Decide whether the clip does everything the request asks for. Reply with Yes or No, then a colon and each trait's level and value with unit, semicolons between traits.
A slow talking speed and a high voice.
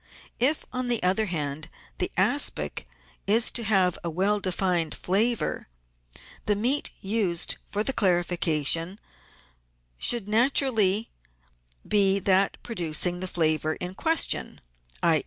Yes: slow, 120 wpm; high, 195 Hz